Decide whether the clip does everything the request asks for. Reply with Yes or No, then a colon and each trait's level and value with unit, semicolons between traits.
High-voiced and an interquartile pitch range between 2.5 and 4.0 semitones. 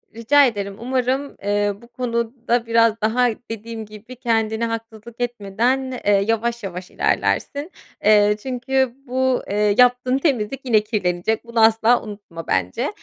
Yes: high, 230 Hz; average, 2.9 semitones